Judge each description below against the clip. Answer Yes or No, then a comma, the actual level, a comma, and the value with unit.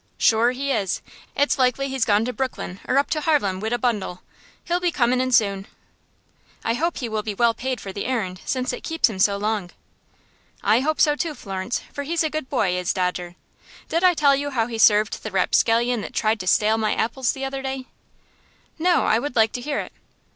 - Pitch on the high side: Yes, high, 240 Hz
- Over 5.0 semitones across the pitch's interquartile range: No, average, 4.6 semitones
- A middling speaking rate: No, fast, 220 wpm